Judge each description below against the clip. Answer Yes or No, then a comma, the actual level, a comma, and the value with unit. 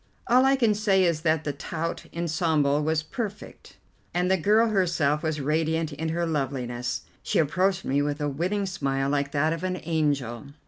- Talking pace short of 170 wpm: No, average, 180 wpm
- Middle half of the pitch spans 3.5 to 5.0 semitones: Yes, average, 4.2 semitones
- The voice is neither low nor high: Yes, medium, 160 Hz